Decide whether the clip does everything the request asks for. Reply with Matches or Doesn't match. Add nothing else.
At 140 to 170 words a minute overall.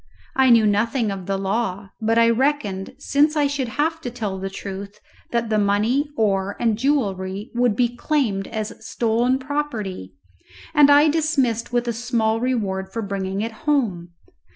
Matches